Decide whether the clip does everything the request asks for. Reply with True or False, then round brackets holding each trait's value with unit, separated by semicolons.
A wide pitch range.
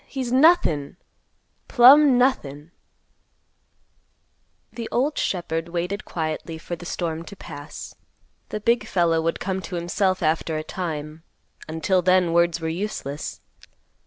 False (4.2 semitones)